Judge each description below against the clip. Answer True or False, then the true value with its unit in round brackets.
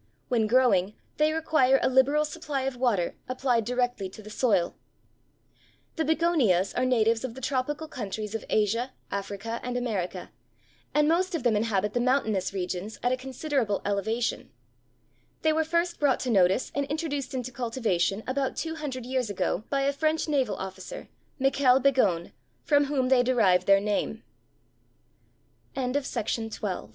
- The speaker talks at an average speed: True (150 wpm)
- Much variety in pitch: False (4.8 semitones)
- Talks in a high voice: True (250 Hz)